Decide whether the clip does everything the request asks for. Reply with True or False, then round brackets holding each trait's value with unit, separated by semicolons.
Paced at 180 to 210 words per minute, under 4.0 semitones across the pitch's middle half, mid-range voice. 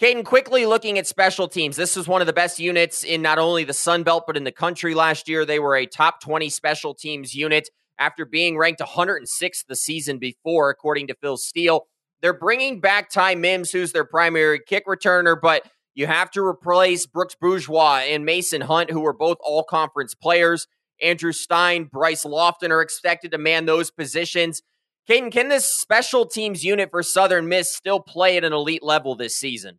True (195 wpm; 2.8 semitones; 170 Hz)